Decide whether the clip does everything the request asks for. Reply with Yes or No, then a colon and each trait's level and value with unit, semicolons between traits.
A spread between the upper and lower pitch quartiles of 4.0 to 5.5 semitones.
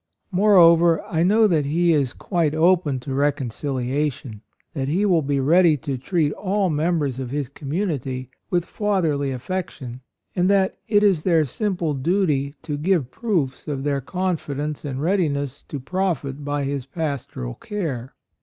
Yes: average, 4.6 semitones